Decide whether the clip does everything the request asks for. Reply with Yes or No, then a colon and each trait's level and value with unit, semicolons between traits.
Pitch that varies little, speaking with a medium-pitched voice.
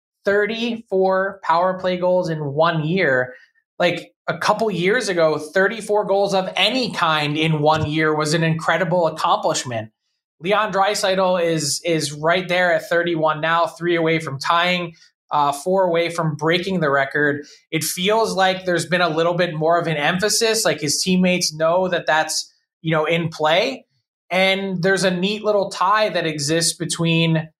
No: average, 3.1 semitones; medium, 170 Hz